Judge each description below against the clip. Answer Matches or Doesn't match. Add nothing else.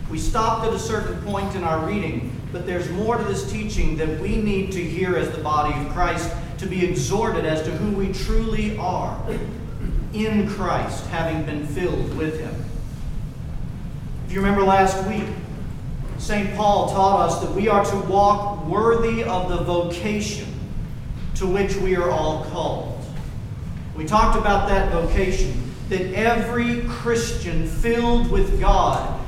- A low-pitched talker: Doesn't match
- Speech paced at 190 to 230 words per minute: Doesn't match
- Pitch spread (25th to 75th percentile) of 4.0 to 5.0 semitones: Matches